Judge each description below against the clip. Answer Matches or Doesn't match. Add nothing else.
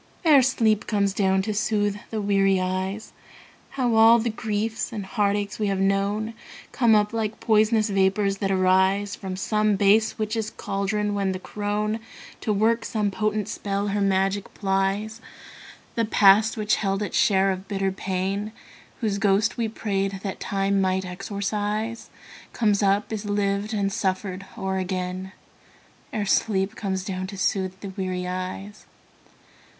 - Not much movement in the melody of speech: Matches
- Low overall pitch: Doesn't match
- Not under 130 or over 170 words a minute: Matches